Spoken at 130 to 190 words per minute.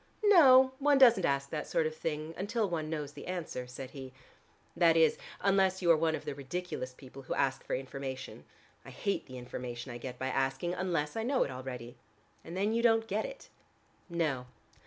No: average, 200 wpm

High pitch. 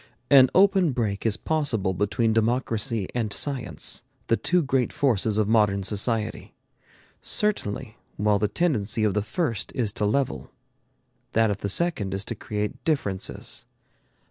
No: low, 110 Hz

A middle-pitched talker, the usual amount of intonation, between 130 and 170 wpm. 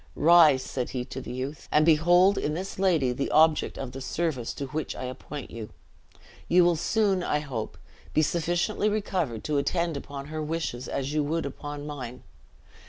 No: medium, 150 Hz; average, 4.1 semitones; average, 180 wpm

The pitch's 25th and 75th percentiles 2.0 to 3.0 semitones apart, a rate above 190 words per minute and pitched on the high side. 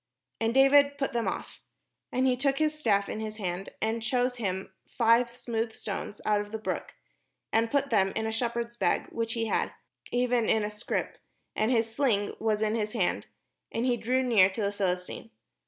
Yes: average, 2.7 semitones; fast, 205 wpm; high, 225 Hz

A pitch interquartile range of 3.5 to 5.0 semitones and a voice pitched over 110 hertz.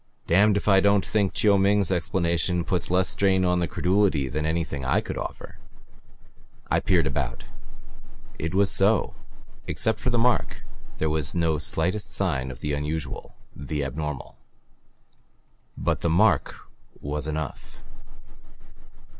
No: average, 4.7 semitones; very low, 85 Hz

